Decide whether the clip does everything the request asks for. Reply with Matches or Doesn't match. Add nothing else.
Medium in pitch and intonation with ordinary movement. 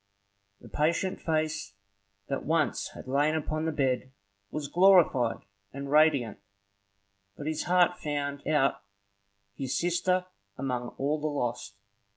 Matches